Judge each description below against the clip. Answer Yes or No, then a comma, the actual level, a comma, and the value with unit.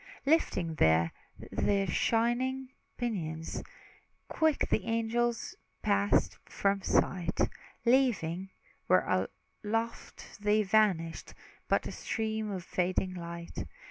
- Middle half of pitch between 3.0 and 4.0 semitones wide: No, average, 4.6 semitones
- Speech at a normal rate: No, slow, 95 wpm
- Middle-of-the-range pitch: No, high, 205 Hz